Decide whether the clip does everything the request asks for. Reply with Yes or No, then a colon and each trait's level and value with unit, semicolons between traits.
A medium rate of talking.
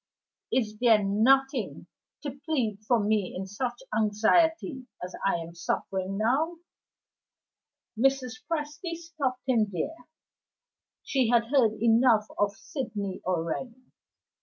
No: slow, 110 wpm